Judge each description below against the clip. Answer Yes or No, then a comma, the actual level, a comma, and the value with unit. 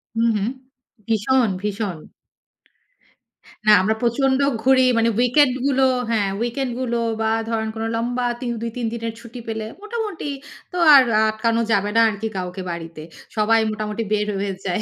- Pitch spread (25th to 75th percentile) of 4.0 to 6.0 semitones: No, average, 2.8 semitones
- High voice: Yes, high, 230 Hz